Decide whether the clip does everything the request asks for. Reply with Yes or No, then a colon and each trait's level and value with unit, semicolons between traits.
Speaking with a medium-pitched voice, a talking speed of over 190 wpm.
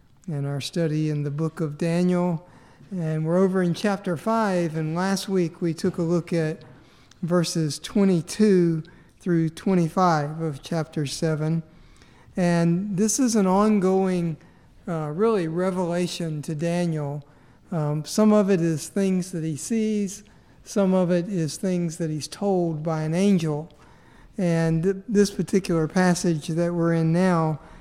No: medium, 170 Hz; average, 145 wpm